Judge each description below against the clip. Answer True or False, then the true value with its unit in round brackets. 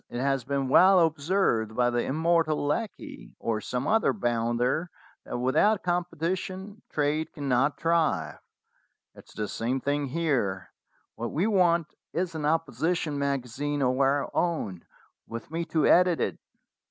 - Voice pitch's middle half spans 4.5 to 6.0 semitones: True (5.2 semitones)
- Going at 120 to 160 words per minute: True (140 wpm)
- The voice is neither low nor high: True (145 Hz)